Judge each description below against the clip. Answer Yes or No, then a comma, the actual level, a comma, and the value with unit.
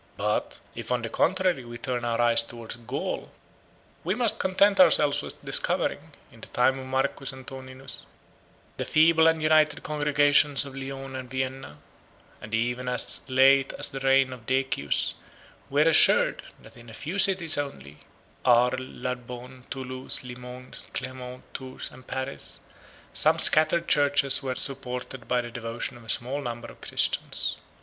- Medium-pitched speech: No, low, 130 Hz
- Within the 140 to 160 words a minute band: Yes, average, 155 wpm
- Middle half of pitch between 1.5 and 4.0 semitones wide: Yes, narrow, 2.6 semitones